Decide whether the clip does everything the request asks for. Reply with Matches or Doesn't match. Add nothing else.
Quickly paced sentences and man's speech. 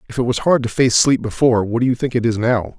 Matches